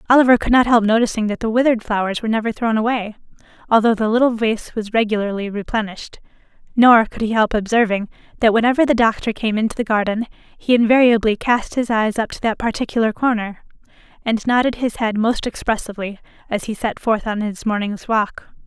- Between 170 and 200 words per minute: Yes, average, 185 wpm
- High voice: Yes, high, 225 Hz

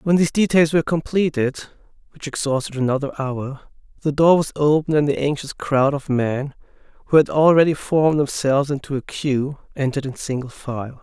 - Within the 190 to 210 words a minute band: No, average, 170 wpm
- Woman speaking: No, male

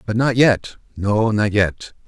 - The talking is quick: No, average, 145 wpm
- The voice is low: Yes, low, 110 Hz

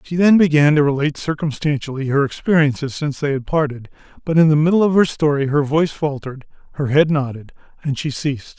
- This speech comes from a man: Yes, male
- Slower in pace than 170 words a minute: No, average, 195 wpm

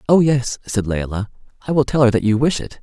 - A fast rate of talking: Yes, fast, 255 wpm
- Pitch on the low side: Yes, low, 125 Hz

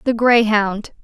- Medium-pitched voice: No, high, 220 Hz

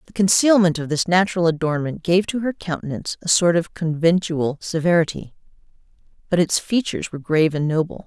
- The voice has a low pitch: No, medium, 170 Hz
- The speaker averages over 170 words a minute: No, average, 165 wpm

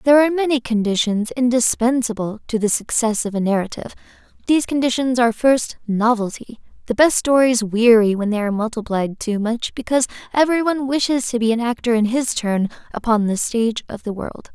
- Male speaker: No, female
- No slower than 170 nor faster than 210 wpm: Yes, average, 175 wpm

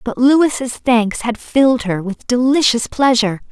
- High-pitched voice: Yes, high, 245 Hz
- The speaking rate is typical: Yes, average, 155 wpm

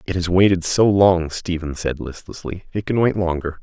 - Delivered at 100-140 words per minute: No, average, 200 wpm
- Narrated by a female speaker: No, male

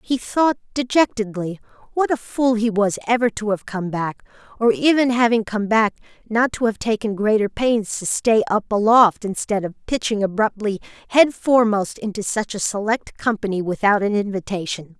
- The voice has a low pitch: No, high, 215 Hz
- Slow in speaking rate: No, average, 170 wpm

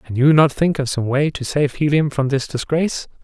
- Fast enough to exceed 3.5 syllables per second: Yes, 5.4 syllables/s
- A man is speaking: Yes, male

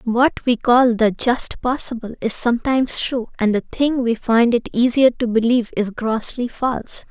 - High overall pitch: Yes, high, 235 Hz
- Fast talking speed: No, average, 175 wpm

